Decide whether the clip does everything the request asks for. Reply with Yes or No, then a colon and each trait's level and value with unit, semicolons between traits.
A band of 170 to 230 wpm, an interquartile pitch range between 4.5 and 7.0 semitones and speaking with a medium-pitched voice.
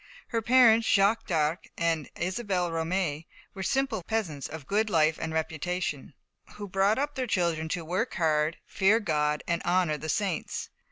No: average, 160 wpm; average, 4.8 semitones; medium, 180 Hz